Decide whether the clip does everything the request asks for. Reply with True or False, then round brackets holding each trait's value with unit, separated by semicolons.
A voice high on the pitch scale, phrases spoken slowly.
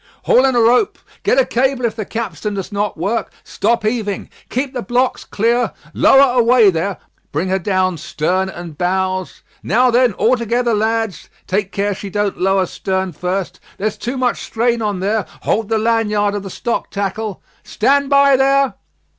False (215 Hz; 175 wpm)